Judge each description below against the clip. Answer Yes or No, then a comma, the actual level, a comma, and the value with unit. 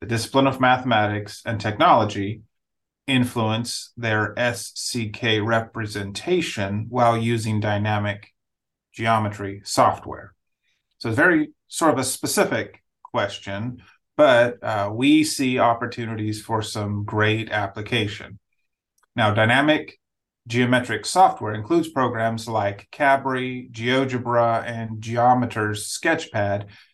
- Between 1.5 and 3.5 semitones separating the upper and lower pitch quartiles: Yes, average, 2.8 semitones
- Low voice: Yes, low, 115 Hz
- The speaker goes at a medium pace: No, slow, 100 wpm